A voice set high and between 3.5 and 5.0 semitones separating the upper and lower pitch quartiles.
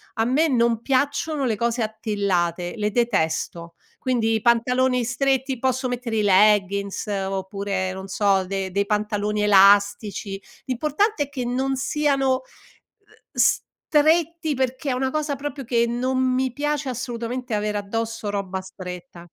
Yes: high, 230 Hz; average, 4.6 semitones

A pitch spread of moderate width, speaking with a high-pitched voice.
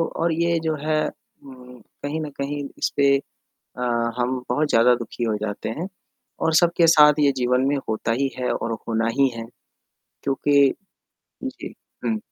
No: average, 3.9 semitones; low, 135 Hz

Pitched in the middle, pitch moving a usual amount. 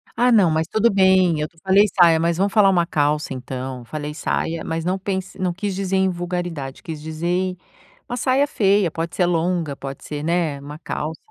Yes: medium, 175 Hz; average, 3.5 semitones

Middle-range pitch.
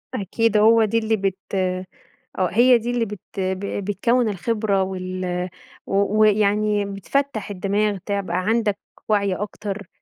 No: high, 205 Hz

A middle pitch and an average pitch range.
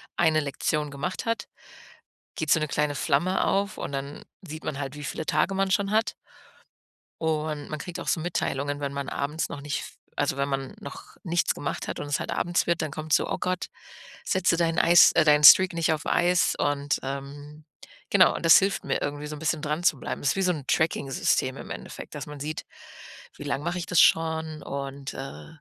Yes: medium, 155 Hz; average, 3.3 semitones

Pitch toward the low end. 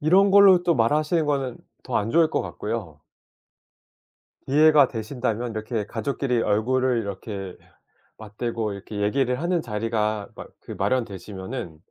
Yes: low, 120 Hz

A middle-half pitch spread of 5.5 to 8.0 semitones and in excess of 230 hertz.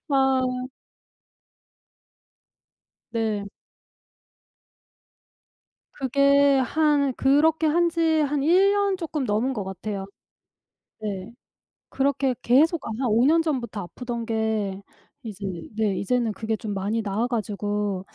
No: average, 5.1 semitones; high, 240 Hz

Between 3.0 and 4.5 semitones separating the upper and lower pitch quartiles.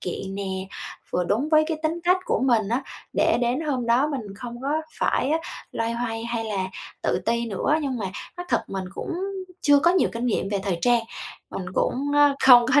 No: average, 5.1 semitones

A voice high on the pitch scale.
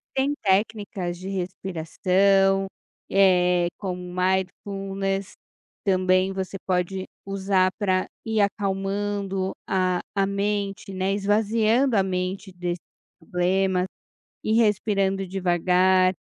Yes: high, 195 Hz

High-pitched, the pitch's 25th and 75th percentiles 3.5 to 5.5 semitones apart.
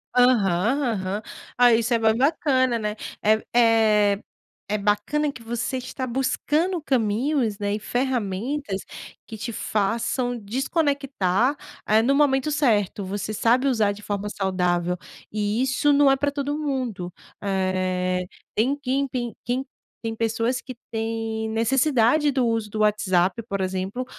Yes: high, 230 Hz; average, 4.3 semitones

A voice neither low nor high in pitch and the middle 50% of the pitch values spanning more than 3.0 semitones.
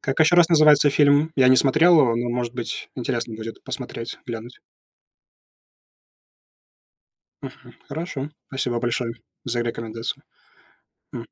No: low, 125 Hz; average, 3.8 semitones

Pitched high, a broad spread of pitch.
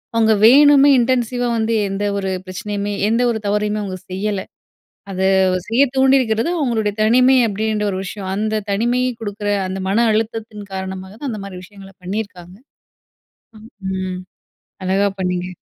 No: high, 210 Hz; average, 3.0 semitones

